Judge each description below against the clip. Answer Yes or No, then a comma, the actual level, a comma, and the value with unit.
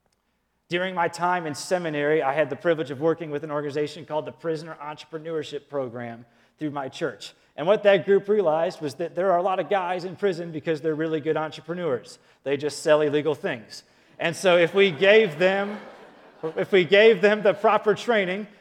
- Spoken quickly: No, average, 195 wpm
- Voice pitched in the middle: Yes, medium, 165 Hz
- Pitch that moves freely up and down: No, average, 4.0 semitones